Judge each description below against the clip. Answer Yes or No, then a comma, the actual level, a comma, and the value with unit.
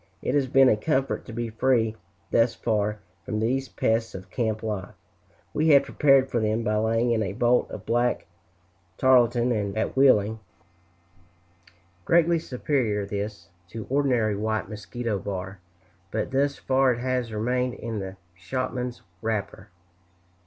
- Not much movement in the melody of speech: No, average, 3.3 semitones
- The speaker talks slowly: No, average, 145 wpm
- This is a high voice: No, low, 115 Hz